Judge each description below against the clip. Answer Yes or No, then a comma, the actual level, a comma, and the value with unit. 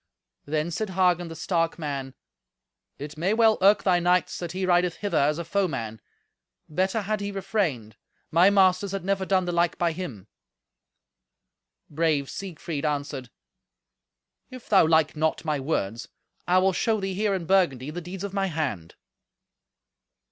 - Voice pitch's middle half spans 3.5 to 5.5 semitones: Yes, average, 4.1 semitones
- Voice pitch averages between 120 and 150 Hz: No, medium, 175 Hz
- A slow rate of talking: No, average, 155 wpm